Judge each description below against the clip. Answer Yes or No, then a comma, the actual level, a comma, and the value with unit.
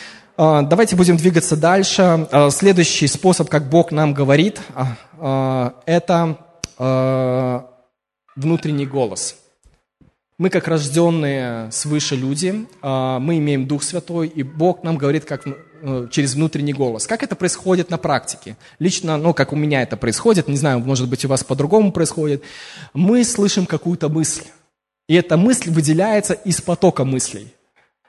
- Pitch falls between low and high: Yes, medium, 155 Hz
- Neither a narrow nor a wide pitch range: Yes, average, 4.0 semitones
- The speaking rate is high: No, average, 130 wpm